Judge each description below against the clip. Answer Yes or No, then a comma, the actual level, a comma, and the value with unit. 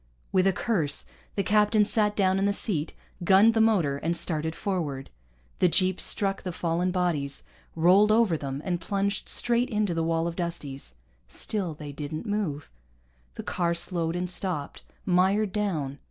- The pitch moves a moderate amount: Yes, average, 3.9 semitones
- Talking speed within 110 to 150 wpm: No, average, 165 wpm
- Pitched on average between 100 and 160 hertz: No, medium, 180 Hz